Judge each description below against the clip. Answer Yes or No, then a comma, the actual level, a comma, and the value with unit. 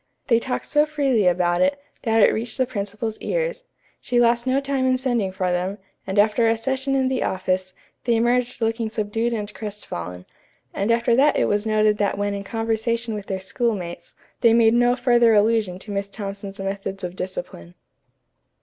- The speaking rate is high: No, average, 185 wpm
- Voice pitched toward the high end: Yes, high, 225 Hz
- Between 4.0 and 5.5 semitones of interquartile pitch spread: No, average, 3.4 semitones